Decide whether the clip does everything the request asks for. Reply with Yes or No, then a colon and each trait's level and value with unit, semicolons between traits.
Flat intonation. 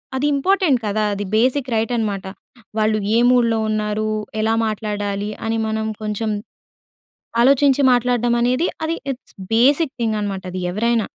No: average, 3.0 semitones